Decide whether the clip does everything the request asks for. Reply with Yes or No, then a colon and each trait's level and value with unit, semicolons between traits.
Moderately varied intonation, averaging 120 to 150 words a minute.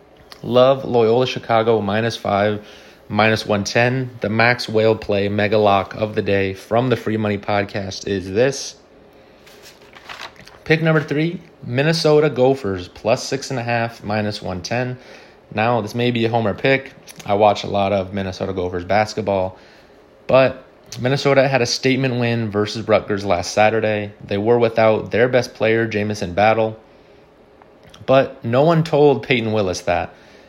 Yes: average, 3.6 semitones; average, 140 wpm